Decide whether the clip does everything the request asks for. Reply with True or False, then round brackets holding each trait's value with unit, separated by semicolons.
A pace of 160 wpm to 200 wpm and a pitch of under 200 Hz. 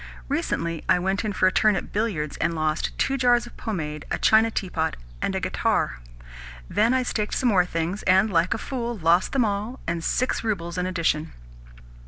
True (195 wpm; 190 Hz)